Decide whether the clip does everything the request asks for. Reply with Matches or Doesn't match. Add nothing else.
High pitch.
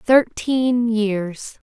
Matches